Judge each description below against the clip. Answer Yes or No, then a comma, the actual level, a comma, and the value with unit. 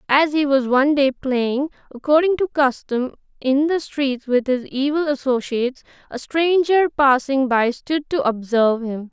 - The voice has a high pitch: Yes, very high, 275 Hz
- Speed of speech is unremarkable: Yes, average, 160 wpm